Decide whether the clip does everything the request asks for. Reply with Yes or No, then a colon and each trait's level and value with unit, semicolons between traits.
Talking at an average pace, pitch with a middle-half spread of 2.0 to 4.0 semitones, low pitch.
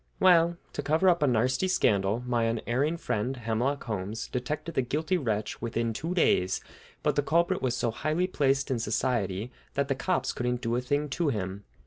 No: average, 185 wpm; average, 5.0 semitones; low, 125 Hz